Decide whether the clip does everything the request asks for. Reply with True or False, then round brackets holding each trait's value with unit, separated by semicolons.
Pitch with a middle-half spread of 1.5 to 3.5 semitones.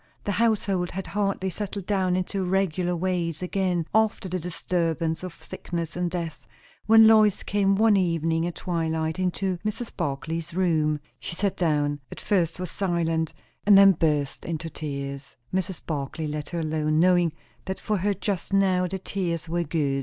True (3.1 semitones)